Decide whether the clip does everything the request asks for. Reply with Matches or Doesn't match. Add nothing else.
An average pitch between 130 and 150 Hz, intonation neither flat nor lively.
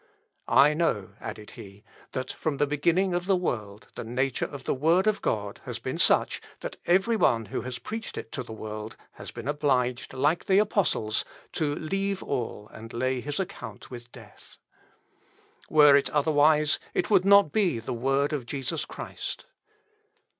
Doesn't match